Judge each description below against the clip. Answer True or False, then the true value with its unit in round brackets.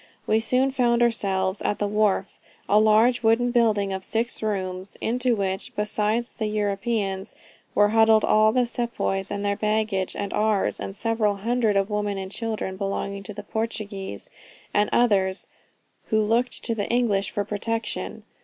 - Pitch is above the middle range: True (210 Hz)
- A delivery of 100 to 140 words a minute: False (155 wpm)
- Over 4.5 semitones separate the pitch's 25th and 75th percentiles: False (2.4 semitones)